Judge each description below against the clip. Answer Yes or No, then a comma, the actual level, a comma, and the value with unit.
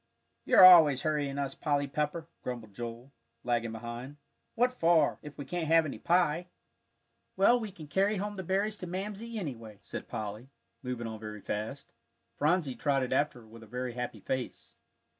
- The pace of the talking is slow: No, average, 170 wpm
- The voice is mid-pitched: Yes, medium, 145 Hz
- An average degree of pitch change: No, wide, 6.7 semitones